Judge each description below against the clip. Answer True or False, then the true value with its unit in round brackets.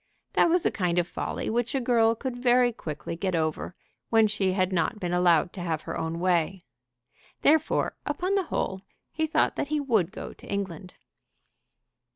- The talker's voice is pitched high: True (195 Hz)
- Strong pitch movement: True (5.8 semitones)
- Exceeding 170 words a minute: True (185 wpm)